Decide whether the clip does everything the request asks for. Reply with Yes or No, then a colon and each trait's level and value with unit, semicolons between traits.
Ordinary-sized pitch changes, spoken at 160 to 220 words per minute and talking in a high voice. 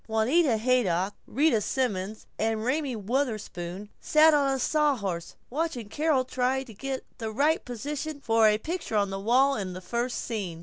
Yes: average, 4.8 semitones; average, 165 wpm; high, 240 Hz